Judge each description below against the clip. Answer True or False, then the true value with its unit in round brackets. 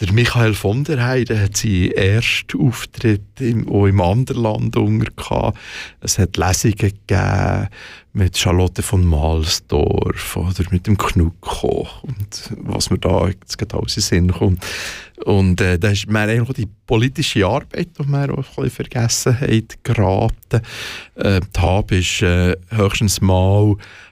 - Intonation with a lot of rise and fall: False (3.4 semitones)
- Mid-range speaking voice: False (105 Hz)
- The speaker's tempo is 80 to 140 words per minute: True (125 wpm)